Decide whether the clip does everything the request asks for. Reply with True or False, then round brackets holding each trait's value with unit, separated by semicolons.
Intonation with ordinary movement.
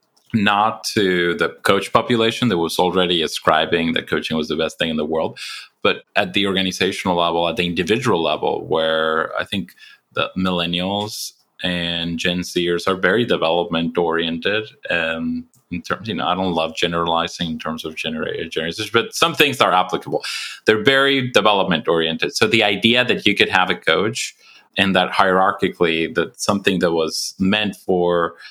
True (3.2 semitones)